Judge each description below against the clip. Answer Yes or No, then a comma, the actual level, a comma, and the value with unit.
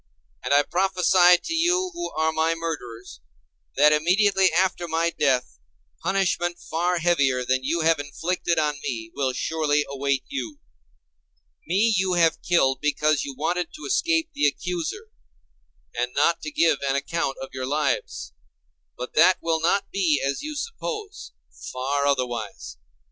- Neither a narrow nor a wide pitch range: Yes, average, 4.7 semitones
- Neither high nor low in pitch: Yes, medium, 160 Hz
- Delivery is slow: No, average, 150 wpm